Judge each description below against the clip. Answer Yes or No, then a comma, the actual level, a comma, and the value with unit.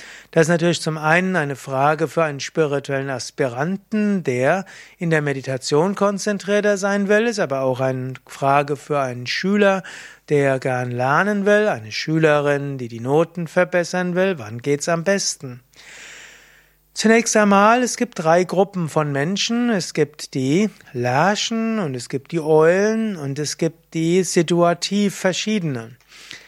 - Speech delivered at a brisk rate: No, average, 145 wpm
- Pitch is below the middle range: No, medium, 165 Hz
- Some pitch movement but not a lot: No, wide, 6.0 semitones